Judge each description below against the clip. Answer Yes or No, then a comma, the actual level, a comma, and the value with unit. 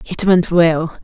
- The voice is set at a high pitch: No, medium, 170 Hz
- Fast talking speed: No, average, 175 wpm